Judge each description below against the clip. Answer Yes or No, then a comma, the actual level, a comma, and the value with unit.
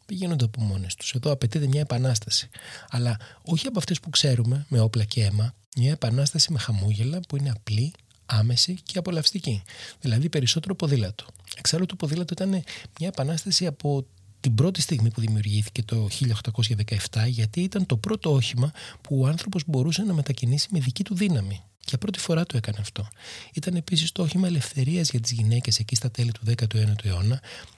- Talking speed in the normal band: No, fast, 175 wpm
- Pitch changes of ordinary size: No, wide, 6.2 semitones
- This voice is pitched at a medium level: No, low, 130 Hz